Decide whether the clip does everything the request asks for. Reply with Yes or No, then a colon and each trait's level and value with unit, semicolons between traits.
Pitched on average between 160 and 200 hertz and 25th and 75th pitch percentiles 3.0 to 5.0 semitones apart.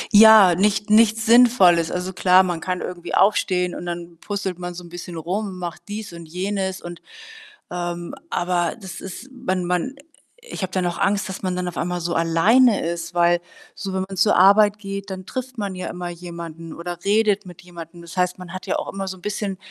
No: medium, 185 Hz; narrow, 2.6 semitones